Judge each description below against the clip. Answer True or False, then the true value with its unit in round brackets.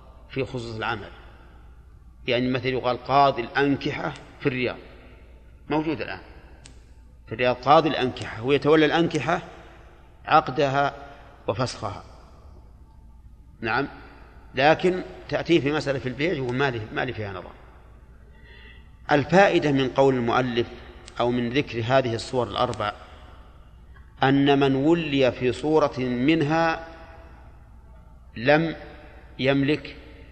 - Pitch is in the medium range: False (125 Hz)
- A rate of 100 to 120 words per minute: True (105 wpm)